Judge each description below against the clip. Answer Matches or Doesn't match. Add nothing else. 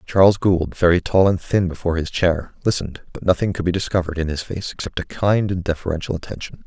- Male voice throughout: Matches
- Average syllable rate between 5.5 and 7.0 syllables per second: Matches